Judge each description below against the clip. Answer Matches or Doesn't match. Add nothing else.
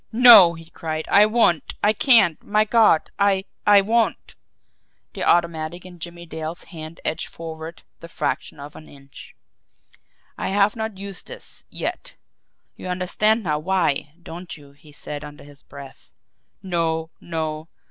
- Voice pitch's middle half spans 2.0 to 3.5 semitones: Doesn't match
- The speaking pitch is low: Doesn't match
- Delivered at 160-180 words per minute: Doesn't match